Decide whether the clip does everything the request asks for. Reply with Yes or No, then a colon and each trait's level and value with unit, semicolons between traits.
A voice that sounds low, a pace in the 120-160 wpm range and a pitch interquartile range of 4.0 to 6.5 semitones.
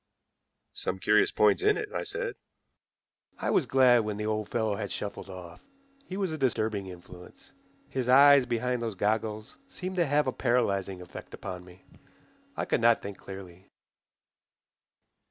Yes: low, 110 Hz; average, 155 wpm; wide, 5.5 semitones